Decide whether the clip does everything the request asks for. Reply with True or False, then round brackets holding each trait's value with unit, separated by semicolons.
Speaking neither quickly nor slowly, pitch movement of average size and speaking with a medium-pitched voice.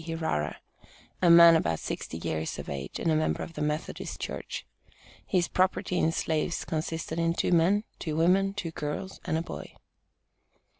False (165 wpm; 2.2 semitones; 165 Hz)